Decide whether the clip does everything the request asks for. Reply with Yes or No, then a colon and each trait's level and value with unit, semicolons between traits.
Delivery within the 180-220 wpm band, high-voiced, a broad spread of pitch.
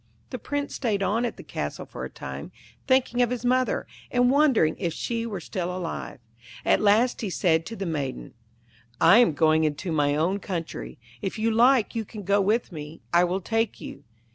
Yes: average, 195 wpm; high, 200 Hz; wide, 6.1 semitones